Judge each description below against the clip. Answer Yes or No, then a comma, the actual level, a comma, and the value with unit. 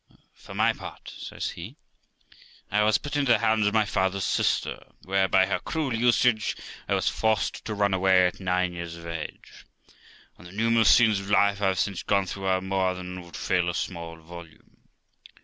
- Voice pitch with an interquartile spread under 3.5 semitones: Yes, average, 2.9 semitones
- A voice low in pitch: Yes, very low, 95 Hz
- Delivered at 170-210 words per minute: Yes, average, 195 wpm